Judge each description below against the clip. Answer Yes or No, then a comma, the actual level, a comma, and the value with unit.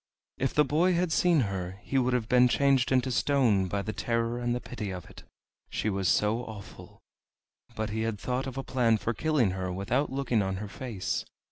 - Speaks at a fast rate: Yes, fast, 210 wpm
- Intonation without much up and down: No, average, 4.6 semitones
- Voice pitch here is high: No, low, 120 Hz